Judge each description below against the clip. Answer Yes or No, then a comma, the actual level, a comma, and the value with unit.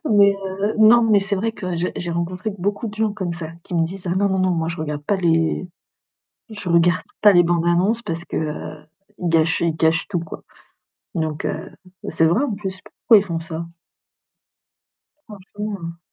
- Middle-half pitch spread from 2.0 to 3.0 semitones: No, average, 3.4 semitones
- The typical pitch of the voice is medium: Yes, medium, 180 Hz